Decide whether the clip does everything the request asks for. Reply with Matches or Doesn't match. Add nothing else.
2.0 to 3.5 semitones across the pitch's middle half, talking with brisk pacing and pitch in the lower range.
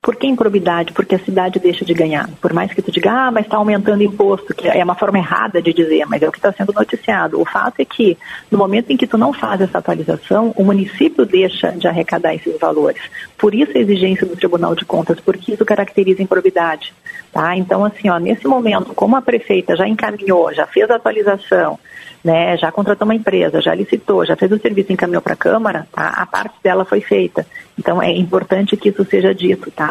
Doesn't match